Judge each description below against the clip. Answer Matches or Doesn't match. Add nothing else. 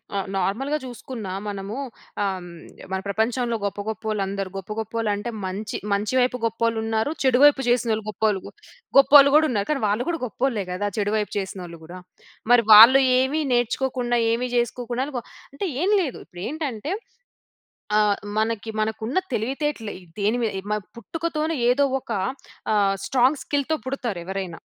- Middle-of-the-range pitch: Doesn't match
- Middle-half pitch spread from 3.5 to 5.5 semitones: Matches